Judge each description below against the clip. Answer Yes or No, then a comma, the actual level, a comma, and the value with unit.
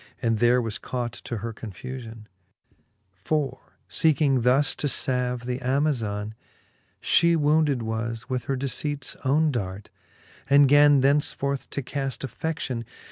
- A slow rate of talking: Yes, slow, 130 wpm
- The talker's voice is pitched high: No, low, 130 Hz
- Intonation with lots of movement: No, average, 3.7 semitones